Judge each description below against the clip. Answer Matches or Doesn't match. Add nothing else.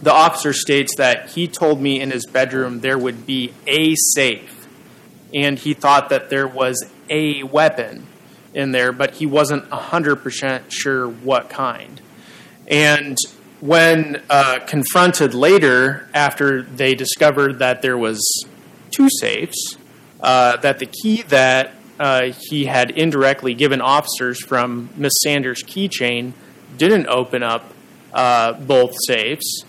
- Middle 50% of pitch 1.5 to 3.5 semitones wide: Matches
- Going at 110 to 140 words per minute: Matches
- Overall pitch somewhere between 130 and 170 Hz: Matches